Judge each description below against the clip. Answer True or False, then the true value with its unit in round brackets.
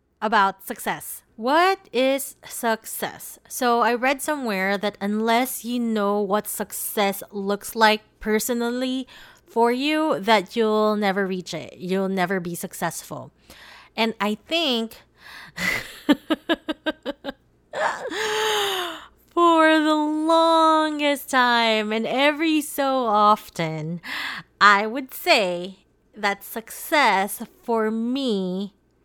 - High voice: True (230 Hz)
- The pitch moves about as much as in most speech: False (6.4 semitones)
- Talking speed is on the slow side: True (95 wpm)